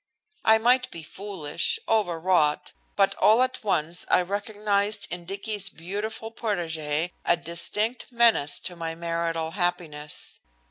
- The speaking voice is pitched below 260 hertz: Yes, medium, 185 Hz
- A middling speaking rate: No, slow, 125 wpm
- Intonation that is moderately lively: Yes, average, 4.5 semitones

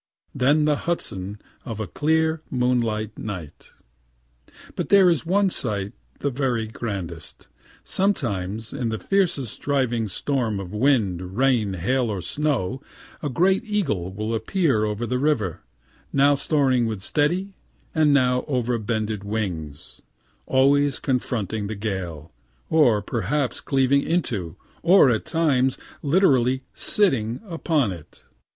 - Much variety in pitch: Yes, wide, 5.7 semitones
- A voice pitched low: Yes, low, 125 Hz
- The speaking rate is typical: No, slow, 125 wpm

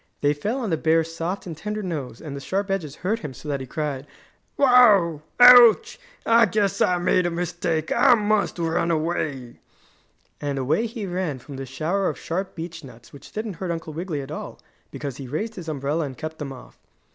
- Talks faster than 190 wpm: Yes, fast, 205 wpm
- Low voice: No, medium, 165 Hz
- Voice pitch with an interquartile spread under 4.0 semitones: No, average, 5.3 semitones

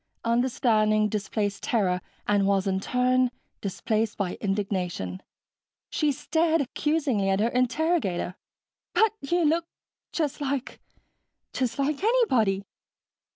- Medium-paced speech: No, slow, 110 wpm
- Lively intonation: Yes, wide, 6.7 semitones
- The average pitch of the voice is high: Yes, high, 235 Hz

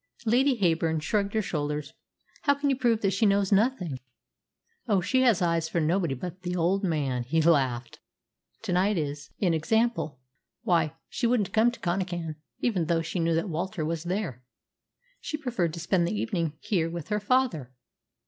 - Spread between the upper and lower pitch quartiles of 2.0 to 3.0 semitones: No, average, 4.8 semitones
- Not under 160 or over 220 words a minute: Yes, average, 175 wpm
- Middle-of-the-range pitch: Yes, medium, 175 Hz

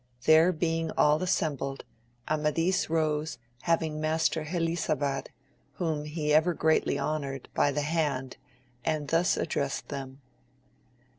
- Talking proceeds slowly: Yes, slow, 115 wpm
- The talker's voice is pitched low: No, medium, 155 Hz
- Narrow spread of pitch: Yes, narrow, 2.0 semitones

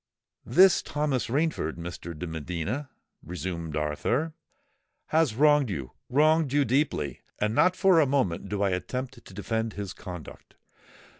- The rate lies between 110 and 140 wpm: Yes, slow, 135 wpm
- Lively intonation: Yes, wide, 8.9 semitones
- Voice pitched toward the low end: Yes, low, 115 Hz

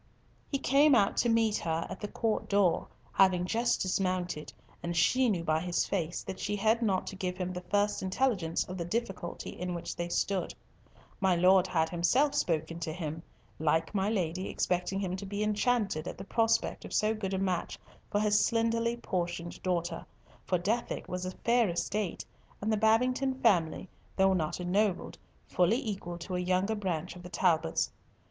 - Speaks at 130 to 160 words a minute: No, average, 180 wpm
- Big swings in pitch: No, average, 3.7 semitones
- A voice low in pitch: No, high, 190 Hz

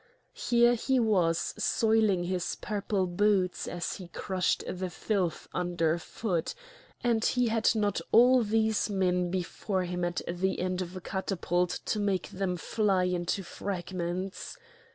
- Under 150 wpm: Yes, average, 140 wpm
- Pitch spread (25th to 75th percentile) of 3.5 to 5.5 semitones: No, average, 3.1 semitones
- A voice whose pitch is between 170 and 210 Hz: Yes, medium, 185 Hz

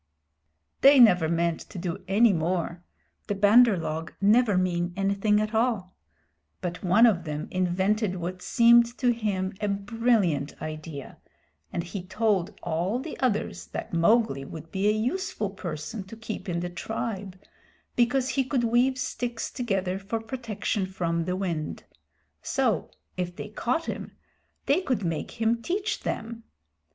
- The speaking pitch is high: Yes, high, 200 Hz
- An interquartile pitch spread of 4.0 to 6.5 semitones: Yes, average, 4.8 semitones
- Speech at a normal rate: Yes, average, 150 wpm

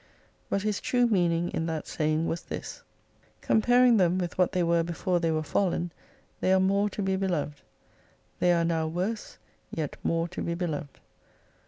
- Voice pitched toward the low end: No, medium, 175 Hz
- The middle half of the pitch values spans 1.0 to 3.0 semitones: Yes, narrow, 2.6 semitones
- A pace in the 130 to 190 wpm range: Yes, average, 175 wpm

